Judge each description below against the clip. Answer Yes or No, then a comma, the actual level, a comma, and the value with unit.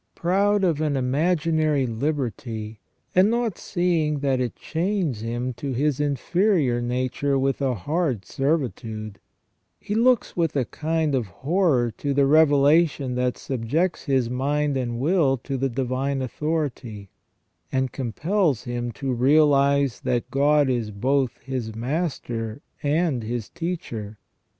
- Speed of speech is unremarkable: No, slow, 130 wpm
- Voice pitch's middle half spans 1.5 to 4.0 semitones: No, average, 4.4 semitones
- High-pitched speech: No, low, 135 Hz